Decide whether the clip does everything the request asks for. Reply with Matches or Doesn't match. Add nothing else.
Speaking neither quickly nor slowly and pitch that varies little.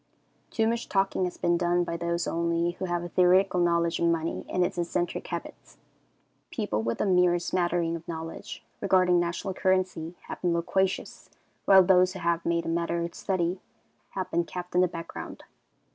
Matches